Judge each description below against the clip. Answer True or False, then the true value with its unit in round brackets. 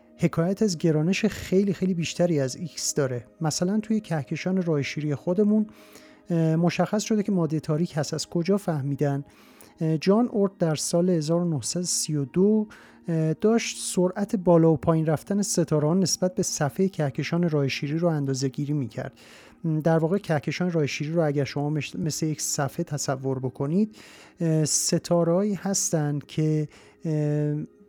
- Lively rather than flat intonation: False (3.7 semitones)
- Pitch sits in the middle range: True (165 Hz)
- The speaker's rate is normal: True (130 wpm)